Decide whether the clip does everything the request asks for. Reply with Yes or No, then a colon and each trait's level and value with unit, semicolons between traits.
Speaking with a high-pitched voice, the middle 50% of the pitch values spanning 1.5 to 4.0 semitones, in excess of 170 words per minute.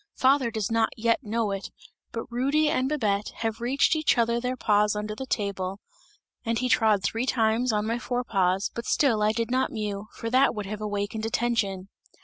Yes: high, 225 Hz; average, 2.8 semitones; average, 195 wpm